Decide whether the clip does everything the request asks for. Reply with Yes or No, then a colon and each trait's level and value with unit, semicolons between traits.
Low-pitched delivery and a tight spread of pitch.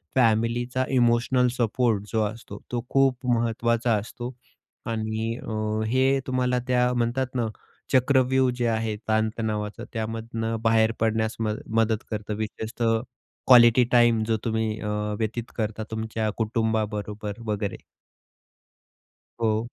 Yes: low, 115 Hz; narrow, 1.8 semitones